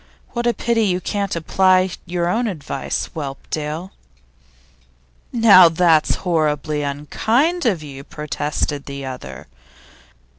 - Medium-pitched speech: Yes, medium, 170 Hz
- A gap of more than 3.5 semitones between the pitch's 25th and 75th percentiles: Yes, average, 5.1 semitones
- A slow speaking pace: Yes, slow, 110 wpm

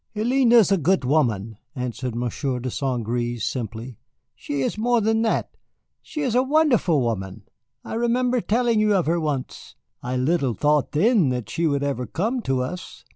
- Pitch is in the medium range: Yes, medium, 150 Hz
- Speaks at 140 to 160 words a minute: No, average, 180 wpm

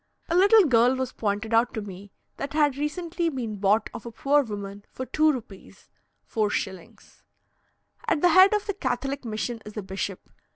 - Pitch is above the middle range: Yes, high, 245 Hz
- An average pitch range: No, wide, 6.2 semitones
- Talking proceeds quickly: No, average, 175 wpm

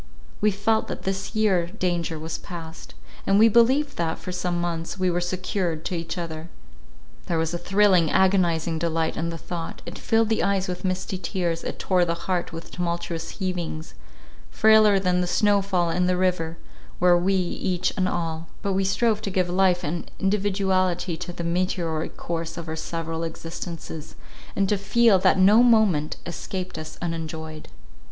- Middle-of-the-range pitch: Yes, medium, 180 Hz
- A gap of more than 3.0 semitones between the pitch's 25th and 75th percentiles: No, average, 2.7 semitones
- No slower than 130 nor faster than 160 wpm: No, average, 175 wpm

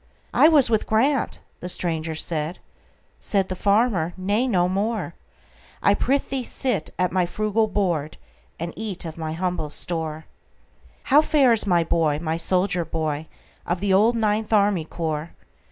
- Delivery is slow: Yes, slow, 120 wpm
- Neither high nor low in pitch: Yes, medium, 180 Hz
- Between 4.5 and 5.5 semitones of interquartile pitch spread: Yes, average, 5.0 semitones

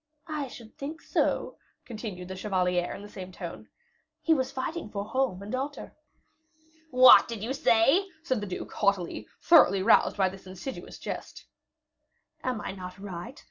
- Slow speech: No, average, 160 wpm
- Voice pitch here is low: No, high, 215 Hz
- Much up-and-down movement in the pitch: Yes, wide, 5.8 semitones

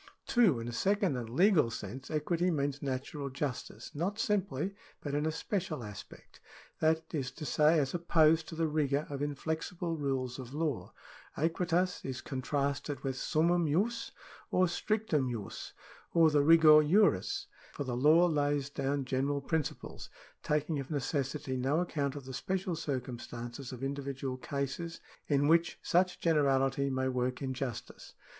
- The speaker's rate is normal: Yes, average, 145 wpm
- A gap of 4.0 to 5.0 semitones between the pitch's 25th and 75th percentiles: No, average, 3.6 semitones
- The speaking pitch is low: No, medium, 145 Hz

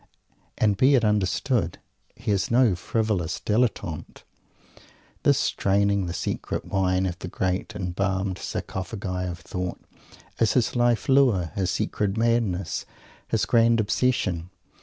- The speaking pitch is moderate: No, low, 100 Hz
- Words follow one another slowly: Yes, slow, 125 wpm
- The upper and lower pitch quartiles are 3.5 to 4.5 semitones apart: Yes, average, 3.9 semitones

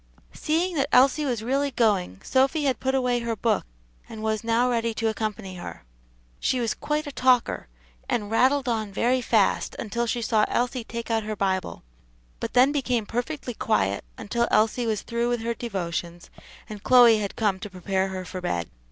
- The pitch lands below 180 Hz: No, high, 230 Hz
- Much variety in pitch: No, average, 3.3 semitones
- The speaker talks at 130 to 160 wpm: No, average, 185 wpm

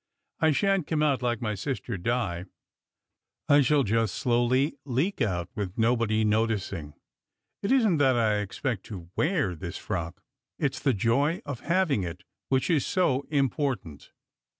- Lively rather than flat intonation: Yes, wide, 5.9 semitones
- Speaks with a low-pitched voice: Yes, low, 120 Hz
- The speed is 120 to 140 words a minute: No, average, 160 wpm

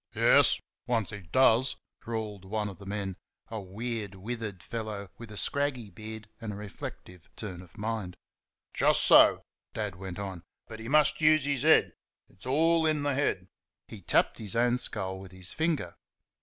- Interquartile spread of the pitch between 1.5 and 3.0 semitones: No, average, 4.0 semitones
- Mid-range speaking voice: No, low, 110 Hz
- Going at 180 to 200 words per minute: No, average, 170 wpm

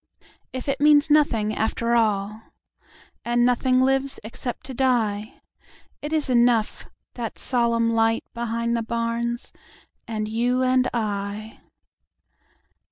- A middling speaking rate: No, slow, 100 wpm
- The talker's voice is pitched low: No, high, 235 Hz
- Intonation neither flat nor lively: No, narrow, 2.3 semitones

